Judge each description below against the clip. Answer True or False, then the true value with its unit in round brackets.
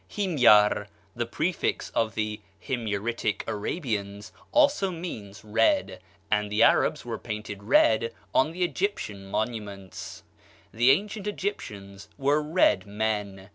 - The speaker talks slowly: True (115 wpm)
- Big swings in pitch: True (7.2 semitones)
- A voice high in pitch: False (110 Hz)